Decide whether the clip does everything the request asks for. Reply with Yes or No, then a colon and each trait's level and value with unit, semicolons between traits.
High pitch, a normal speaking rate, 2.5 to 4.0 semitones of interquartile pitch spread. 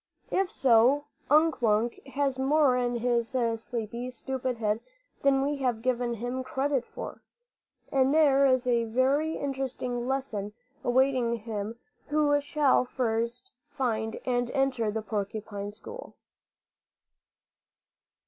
No: very high, 250 Hz; slow, 120 wpm; average, 2.9 semitones